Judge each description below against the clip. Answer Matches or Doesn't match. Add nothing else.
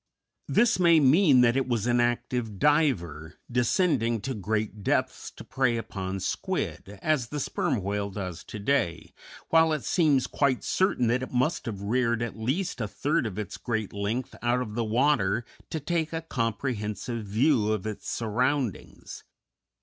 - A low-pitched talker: Matches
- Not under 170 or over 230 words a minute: Doesn't match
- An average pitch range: Matches